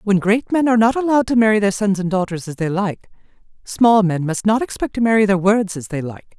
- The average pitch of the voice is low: No, high, 205 Hz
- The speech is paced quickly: Yes, fast, 255 wpm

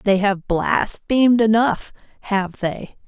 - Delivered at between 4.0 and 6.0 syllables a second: No, 3.6 syllables/s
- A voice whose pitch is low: No, high, 210 Hz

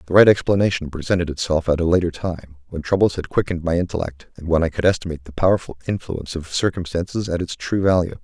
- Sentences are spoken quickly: Yes, fast, 210 wpm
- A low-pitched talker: Yes, very low, 85 Hz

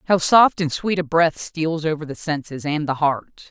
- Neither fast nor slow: No, fast, 225 wpm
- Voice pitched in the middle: Yes, medium, 160 Hz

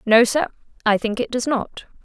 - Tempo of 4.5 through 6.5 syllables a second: Yes, 5.0 syllables/s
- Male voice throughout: No, female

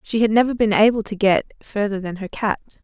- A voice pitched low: No, high, 210 Hz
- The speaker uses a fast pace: Yes, fast, 235 wpm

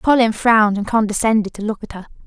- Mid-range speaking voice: No, high, 215 Hz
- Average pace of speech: No, fast, 210 wpm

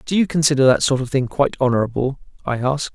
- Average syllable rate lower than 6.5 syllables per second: No, 6.9 syllables/s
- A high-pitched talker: No, low, 135 Hz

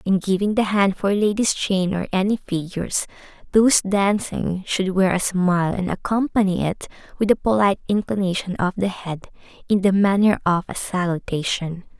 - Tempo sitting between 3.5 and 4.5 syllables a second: No, 5.0 syllables/s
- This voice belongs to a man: No, female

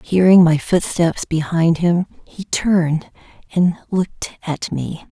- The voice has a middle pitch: Yes, medium, 170 Hz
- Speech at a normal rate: No, slow, 130 wpm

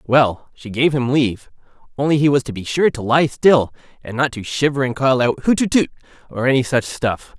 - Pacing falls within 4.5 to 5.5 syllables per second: Yes, 5.3 syllables/s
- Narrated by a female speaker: No, male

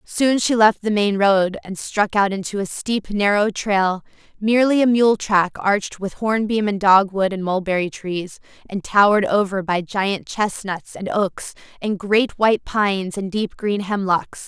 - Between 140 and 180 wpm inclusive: Yes, average, 175 wpm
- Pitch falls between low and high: No, high, 200 Hz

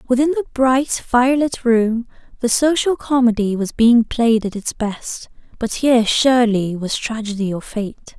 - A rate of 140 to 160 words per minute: Yes, average, 155 wpm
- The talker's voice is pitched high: Yes, high, 235 Hz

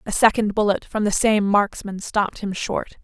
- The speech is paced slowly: No, average, 200 wpm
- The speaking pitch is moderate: No, high, 205 Hz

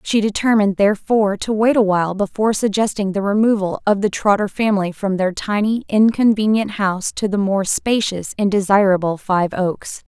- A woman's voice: Yes, female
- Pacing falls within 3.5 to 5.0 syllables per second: No, 5.4 syllables/s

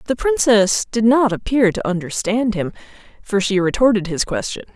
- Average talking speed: Yes, average, 165 wpm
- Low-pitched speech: No, high, 220 Hz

